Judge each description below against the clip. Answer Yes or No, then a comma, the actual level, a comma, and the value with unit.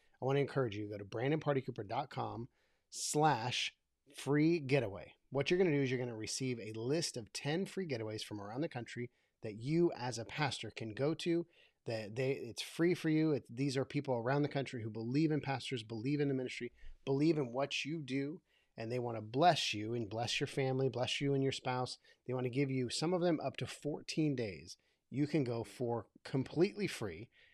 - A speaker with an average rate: No, fast, 215 wpm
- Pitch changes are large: No, average, 3.9 semitones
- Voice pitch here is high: No, low, 135 Hz